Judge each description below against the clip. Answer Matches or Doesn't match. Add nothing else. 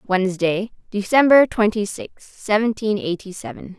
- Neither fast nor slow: Doesn't match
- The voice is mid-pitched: Doesn't match